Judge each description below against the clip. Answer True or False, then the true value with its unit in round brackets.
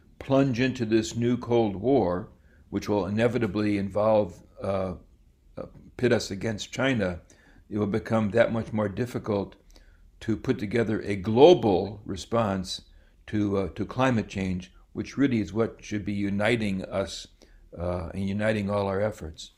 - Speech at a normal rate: True (145 wpm)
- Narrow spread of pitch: False (3.5 semitones)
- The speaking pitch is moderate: False (105 Hz)